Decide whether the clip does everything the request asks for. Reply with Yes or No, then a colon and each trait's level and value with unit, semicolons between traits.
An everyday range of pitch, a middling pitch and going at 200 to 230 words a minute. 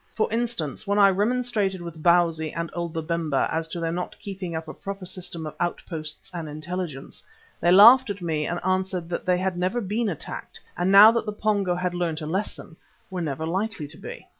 Yes: average, 3.5 semitones; medium, 180 Hz; fast, 205 wpm